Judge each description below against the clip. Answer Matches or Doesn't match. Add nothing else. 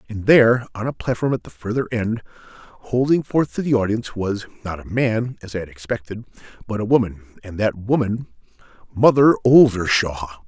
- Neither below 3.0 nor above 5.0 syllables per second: Doesn't match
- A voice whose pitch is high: Doesn't match